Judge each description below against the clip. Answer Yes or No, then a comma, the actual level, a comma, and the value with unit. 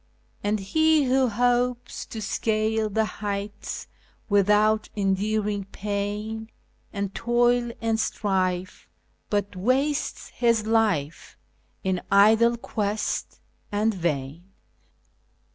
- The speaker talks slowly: Yes, slow, 95 wpm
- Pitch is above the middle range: Yes, high, 215 Hz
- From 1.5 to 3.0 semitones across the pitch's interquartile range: Yes, narrow, 2.4 semitones